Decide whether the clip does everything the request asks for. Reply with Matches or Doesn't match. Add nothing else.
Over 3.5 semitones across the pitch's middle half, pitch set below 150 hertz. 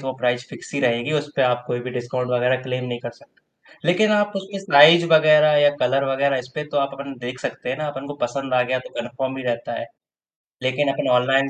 Doesn't match